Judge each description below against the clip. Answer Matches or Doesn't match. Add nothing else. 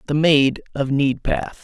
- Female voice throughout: Doesn't match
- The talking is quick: Doesn't match